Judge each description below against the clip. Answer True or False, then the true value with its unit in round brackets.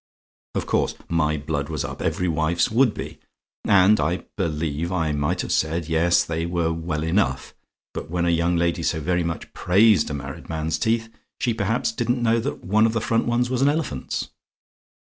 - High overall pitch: False (85 Hz)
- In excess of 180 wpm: True (190 wpm)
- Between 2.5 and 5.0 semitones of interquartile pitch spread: False (5.6 semitones)